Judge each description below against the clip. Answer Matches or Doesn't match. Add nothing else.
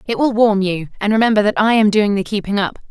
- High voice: Matches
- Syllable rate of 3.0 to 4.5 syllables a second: Doesn't match